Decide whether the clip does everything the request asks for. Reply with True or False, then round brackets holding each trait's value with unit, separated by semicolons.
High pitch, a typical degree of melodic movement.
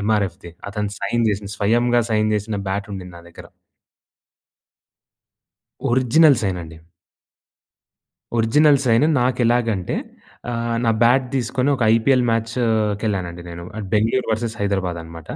False (110 Hz; 3.3 semitones)